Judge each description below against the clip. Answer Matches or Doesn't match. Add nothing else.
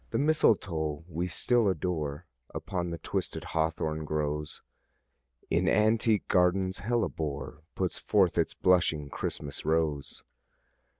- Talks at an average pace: Doesn't match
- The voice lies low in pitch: Matches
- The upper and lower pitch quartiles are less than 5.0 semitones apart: Matches